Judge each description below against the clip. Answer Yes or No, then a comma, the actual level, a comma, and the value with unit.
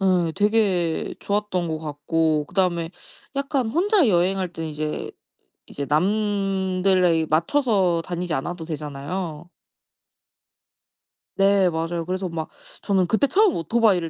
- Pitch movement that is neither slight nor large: Yes, average, 3.6 semitones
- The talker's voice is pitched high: No, medium, 180 Hz